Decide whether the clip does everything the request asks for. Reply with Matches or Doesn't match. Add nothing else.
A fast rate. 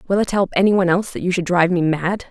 Matches